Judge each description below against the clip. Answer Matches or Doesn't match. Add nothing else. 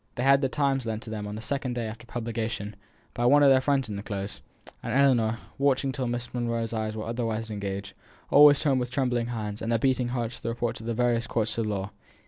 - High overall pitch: Doesn't match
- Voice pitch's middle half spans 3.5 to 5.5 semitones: Doesn't match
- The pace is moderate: Doesn't match